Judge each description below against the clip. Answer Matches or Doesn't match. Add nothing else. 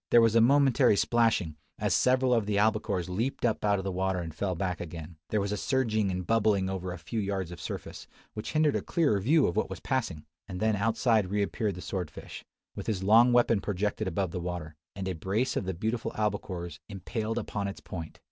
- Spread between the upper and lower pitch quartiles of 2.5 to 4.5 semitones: Matches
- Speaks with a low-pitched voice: Matches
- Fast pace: Matches